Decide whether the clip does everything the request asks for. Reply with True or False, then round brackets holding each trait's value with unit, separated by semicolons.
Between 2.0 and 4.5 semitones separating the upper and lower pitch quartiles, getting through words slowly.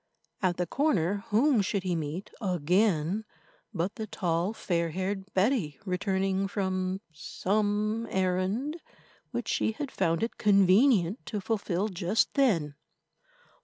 True (3.1 semitones; 125 wpm)